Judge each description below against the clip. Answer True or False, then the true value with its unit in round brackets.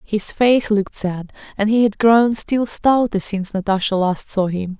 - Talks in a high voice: True (210 Hz)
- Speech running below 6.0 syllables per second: True (4.5 syllables/s)